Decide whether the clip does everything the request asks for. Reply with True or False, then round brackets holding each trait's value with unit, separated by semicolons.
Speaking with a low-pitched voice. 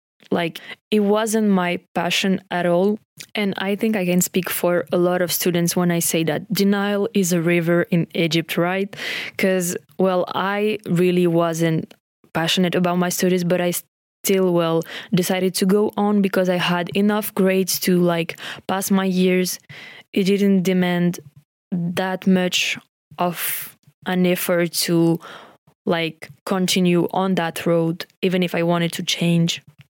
False (180 Hz)